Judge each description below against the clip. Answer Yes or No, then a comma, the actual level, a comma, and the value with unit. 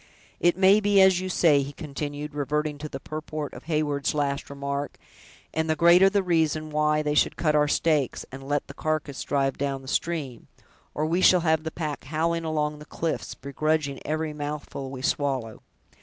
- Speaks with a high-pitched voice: No, medium, 150 Hz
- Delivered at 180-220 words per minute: Yes, average, 185 wpm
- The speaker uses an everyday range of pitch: No, narrow, 2.1 semitones